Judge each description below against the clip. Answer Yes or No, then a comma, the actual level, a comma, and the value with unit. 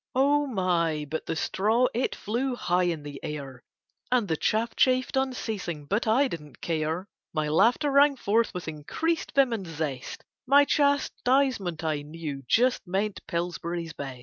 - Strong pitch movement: Yes, wide, 8.2 semitones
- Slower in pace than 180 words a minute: Yes, average, 155 wpm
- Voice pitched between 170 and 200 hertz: Yes, high, 190 Hz